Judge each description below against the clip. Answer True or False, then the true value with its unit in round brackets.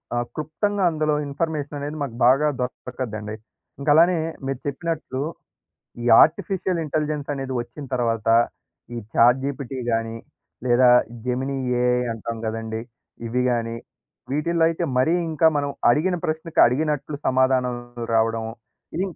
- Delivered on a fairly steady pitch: False (4.2 semitones)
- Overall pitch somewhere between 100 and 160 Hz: True (135 Hz)